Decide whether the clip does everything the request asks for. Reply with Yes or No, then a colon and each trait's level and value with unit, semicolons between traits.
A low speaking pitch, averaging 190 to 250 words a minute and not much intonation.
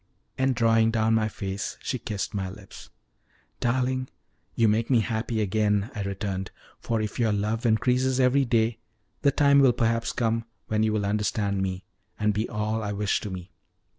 No: low, 110 Hz; average, 175 wpm; narrow, 2.3 semitones